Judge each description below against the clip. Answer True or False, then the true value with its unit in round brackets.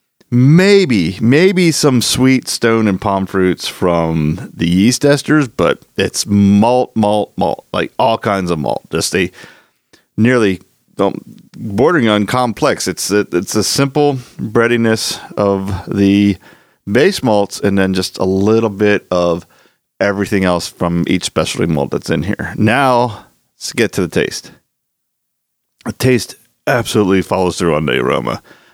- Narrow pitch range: False (4.6 semitones)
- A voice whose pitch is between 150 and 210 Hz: False (105 Hz)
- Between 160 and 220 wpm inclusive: False (145 wpm)